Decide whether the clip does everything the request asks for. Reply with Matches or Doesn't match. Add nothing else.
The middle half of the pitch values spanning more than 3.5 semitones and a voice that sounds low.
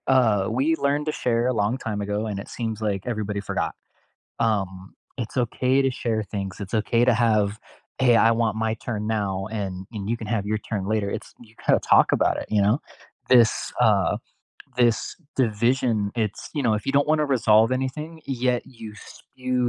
Doesn't match